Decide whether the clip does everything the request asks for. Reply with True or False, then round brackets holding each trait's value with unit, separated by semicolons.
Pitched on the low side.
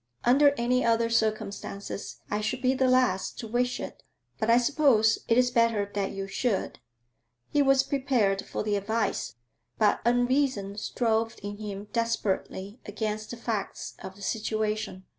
False (225 Hz)